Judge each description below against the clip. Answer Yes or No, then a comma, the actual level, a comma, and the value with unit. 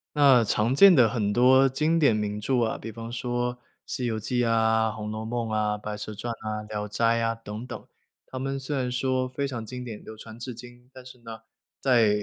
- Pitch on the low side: Yes, low, 120 Hz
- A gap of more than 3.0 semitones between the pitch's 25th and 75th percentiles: No, narrow, 2.6 semitones